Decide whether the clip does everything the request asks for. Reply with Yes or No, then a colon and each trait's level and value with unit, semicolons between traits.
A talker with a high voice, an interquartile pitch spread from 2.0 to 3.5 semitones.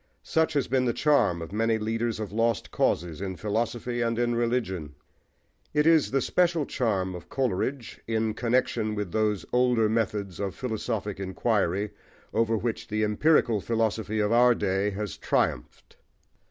No: low, 110 Hz; average, 2.8 semitones